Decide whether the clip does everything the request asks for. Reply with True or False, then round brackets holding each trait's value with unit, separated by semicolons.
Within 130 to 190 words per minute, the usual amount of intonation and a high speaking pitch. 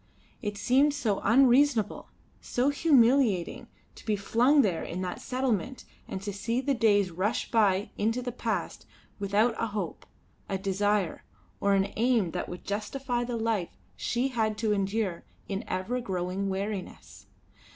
True (150 wpm; 3.9 semitones; 215 Hz)